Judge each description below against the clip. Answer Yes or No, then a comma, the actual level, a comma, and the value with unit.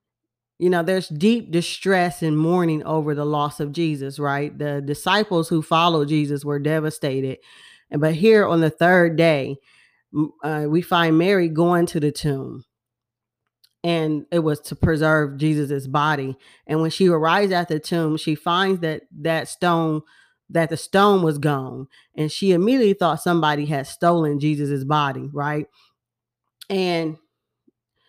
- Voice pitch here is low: No, medium, 155 Hz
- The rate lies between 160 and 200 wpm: No, average, 150 wpm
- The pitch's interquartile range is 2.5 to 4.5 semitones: Yes, average, 2.8 semitones